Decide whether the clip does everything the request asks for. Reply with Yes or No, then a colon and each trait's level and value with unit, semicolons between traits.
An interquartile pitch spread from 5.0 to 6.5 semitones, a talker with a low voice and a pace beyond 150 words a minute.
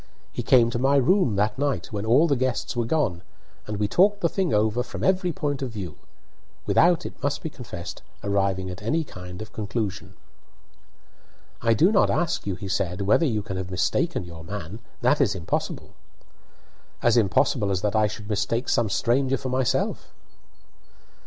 Yes: wide, 5.6 semitones; low, 110 Hz; average, 180 wpm